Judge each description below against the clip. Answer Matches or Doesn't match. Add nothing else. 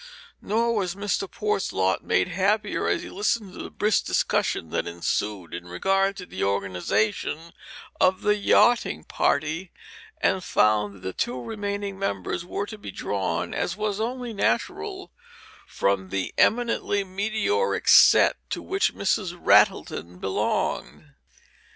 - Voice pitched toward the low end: Doesn't match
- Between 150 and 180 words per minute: Doesn't match